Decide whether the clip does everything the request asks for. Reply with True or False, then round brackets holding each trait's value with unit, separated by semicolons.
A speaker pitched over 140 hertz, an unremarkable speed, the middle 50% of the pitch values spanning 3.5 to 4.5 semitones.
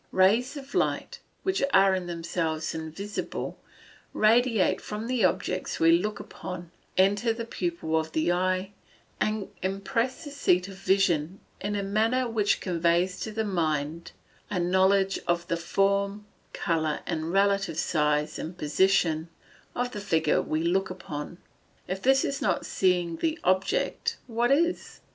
True (190 Hz; 145 wpm; 3.9 semitones)